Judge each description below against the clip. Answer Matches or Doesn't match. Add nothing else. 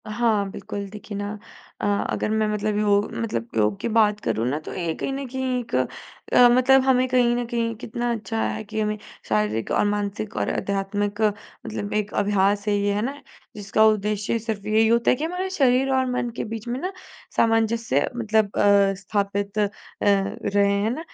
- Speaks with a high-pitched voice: Matches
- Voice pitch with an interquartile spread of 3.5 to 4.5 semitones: Doesn't match